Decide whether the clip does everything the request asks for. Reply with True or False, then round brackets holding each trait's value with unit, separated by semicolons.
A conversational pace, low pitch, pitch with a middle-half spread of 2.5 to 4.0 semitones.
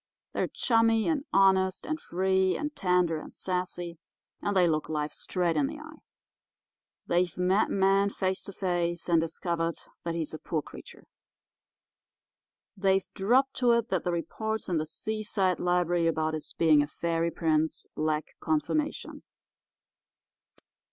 False (145 wpm; 180 Hz; 3.0 semitones)